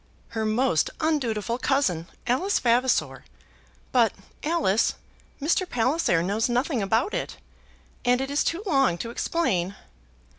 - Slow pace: Yes, slow, 120 wpm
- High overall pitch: Yes, high, 245 Hz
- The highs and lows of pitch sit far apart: No, average, 4.8 semitones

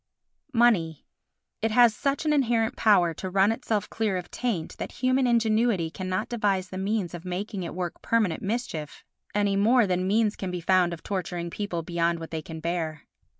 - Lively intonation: No, average, 4.5 semitones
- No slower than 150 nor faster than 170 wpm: No, average, 185 wpm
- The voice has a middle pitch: No, high, 195 Hz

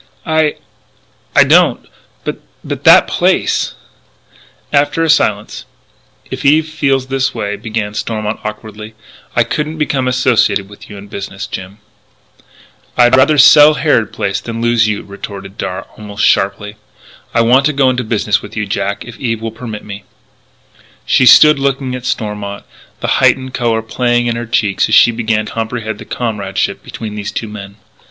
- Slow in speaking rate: No, average, 165 wpm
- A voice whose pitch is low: Yes, low, 115 Hz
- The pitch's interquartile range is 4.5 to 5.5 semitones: No, average, 3.9 semitones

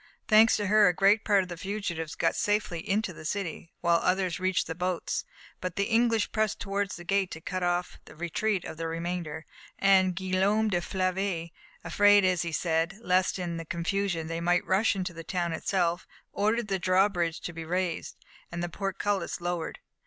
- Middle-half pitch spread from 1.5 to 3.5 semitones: Yes, average, 2.8 semitones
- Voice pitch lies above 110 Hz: Yes, medium, 185 Hz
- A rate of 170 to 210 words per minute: Yes, average, 190 wpm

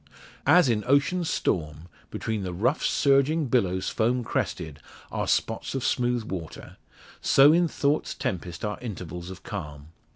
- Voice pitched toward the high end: No, low, 110 Hz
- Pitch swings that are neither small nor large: No, wide, 7.5 semitones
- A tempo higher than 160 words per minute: No, average, 140 wpm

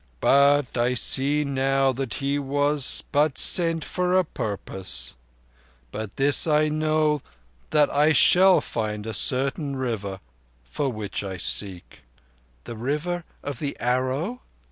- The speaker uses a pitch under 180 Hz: Yes, medium, 140 Hz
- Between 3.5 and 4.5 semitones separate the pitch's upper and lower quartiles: Yes, average, 4.1 semitones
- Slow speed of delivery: Yes, slow, 130 wpm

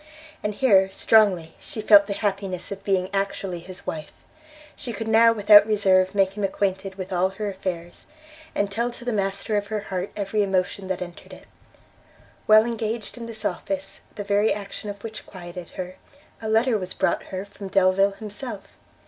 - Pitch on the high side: Yes, high, 200 Hz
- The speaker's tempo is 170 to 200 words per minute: Yes, average, 180 wpm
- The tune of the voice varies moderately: No, narrow, 2.2 semitones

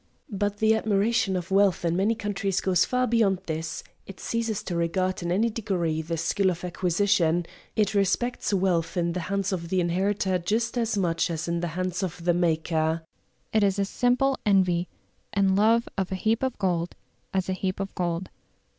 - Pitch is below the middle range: No, high, 190 Hz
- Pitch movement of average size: Yes, average, 3.0 semitones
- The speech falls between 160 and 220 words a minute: Yes, average, 190 wpm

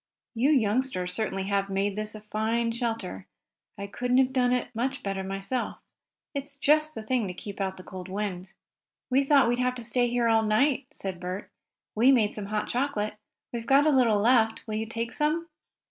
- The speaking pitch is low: No, high, 225 Hz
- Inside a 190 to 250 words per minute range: Yes, average, 195 wpm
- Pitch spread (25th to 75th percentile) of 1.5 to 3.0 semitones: No, average, 4.1 semitones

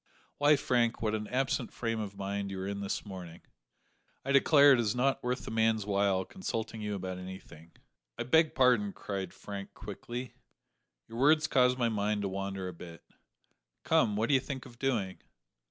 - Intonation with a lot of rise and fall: No, average, 4.3 semitones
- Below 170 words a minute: No, average, 185 wpm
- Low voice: Yes, low, 110 Hz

